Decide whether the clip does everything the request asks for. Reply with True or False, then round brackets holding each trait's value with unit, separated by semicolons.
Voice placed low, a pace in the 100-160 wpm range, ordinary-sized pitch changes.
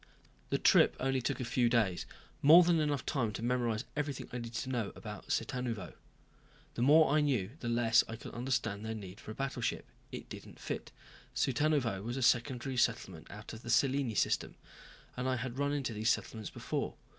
False (120 Hz; 195 wpm; 3.1 semitones)